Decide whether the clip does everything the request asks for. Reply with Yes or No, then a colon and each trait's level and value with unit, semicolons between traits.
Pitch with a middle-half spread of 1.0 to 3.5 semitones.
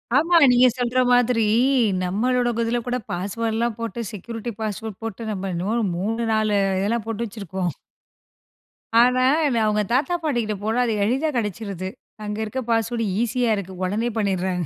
Yes: average, 2.9 semitones